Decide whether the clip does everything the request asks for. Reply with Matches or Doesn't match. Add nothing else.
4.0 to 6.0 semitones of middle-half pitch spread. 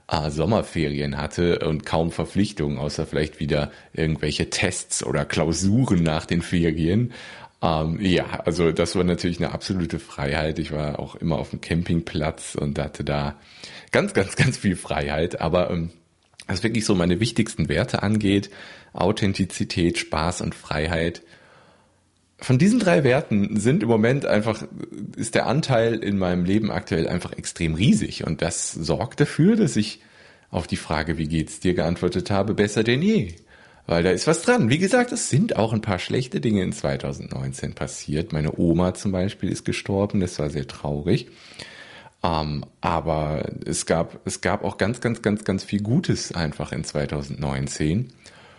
Matches